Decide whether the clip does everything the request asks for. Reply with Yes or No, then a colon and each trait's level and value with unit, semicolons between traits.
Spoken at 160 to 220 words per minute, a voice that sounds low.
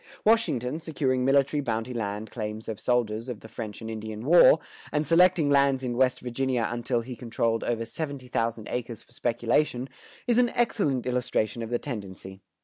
Yes: average, 170 wpm; low, 125 Hz